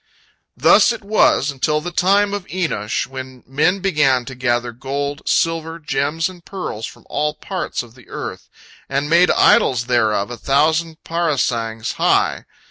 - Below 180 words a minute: Yes, average, 150 wpm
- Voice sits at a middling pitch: Yes, medium, 145 Hz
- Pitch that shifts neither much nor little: Yes, average, 5.0 semitones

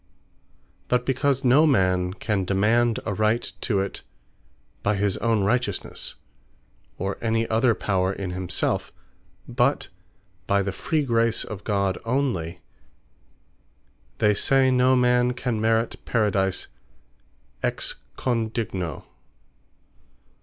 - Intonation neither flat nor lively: Yes, average, 4.0 semitones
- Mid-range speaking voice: No, low, 110 Hz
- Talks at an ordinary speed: No, slow, 110 wpm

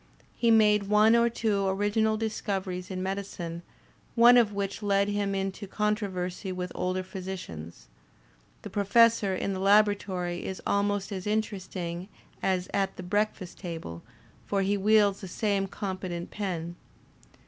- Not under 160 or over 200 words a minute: No, average, 150 wpm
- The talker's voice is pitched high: Yes, high, 195 Hz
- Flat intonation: Yes, narrow, 2.2 semitones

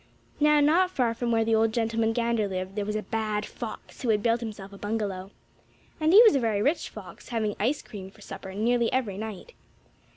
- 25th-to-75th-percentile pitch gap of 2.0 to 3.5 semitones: Yes, average, 2.7 semitones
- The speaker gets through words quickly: Yes, fast, 215 wpm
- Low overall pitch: No, high, 225 Hz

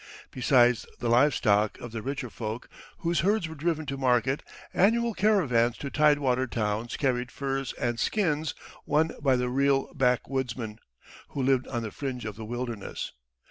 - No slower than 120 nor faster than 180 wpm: Yes, average, 160 wpm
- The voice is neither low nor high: No, low, 130 Hz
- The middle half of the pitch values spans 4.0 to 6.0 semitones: No, average, 3.6 semitones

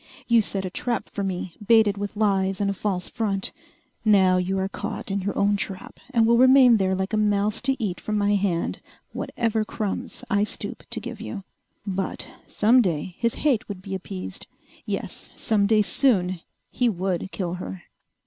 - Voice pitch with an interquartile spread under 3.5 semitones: Yes, average, 2.7 semitones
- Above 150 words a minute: Yes, average, 185 wpm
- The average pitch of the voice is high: Yes, high, 200 Hz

